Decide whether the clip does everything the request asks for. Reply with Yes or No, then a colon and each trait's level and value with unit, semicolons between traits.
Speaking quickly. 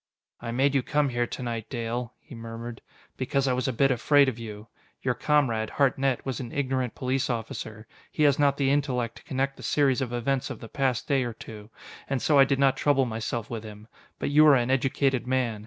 Yes: fast, 220 wpm